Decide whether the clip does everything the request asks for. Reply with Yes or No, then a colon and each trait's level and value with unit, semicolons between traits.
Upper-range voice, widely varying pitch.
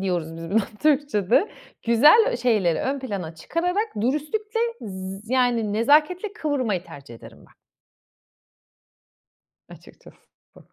Yes: high, 235 Hz; wide, 8.0 semitones